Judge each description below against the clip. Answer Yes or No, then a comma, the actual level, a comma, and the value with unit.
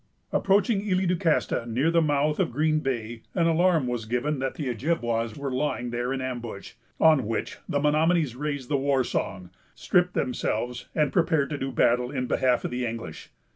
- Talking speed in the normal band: Yes, average, 185 wpm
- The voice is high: No, low, 135 Hz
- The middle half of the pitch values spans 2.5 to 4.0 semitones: No, average, 4.5 semitones